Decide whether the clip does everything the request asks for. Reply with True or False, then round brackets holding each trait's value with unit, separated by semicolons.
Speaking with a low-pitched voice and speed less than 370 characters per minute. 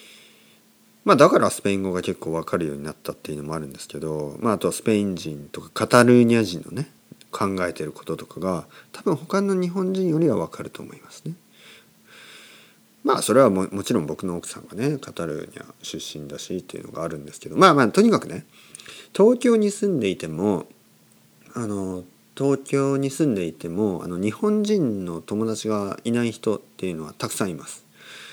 False (100 Hz; 380 characters per minute)